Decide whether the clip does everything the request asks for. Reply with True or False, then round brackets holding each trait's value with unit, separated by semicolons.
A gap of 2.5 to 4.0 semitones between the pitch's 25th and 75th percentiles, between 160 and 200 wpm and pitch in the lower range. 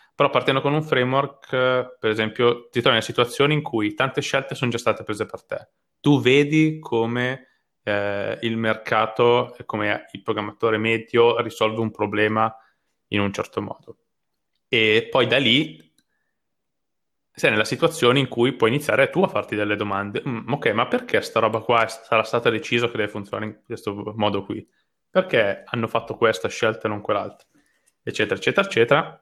True (2.9 semitones; 170 wpm; 115 Hz)